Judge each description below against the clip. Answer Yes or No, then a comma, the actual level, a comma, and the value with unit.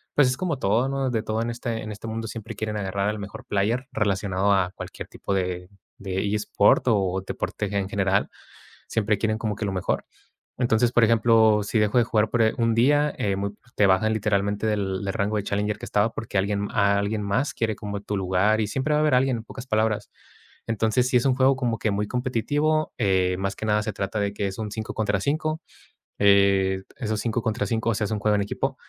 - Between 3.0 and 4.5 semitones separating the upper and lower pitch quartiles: No, narrow, 2.5 semitones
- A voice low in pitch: Yes, low, 105 Hz